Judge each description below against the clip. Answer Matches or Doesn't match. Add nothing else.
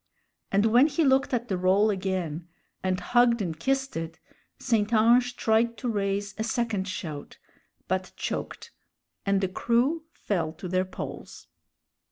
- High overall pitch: Matches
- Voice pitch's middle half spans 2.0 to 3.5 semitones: Doesn't match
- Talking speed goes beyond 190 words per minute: Doesn't match